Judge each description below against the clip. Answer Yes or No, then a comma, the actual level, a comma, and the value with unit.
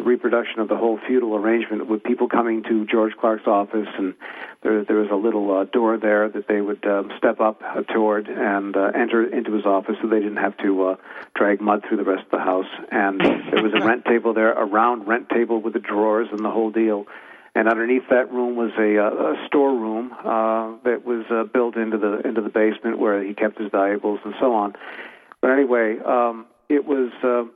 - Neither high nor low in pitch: No, low, 110 Hz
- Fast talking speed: Yes, fast, 220 wpm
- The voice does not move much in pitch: Yes, narrow, 1.9 semitones